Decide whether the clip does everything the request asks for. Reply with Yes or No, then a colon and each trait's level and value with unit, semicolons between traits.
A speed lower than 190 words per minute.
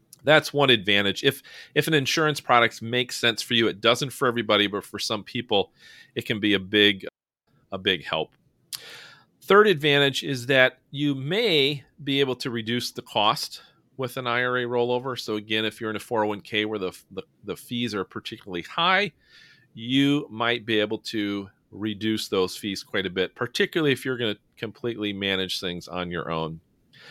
Yes: average, 180 wpm